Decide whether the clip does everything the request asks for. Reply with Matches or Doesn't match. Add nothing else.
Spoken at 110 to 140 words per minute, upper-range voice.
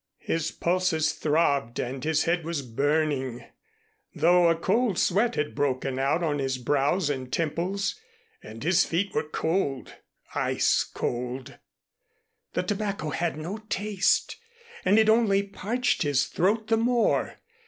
Doesn't match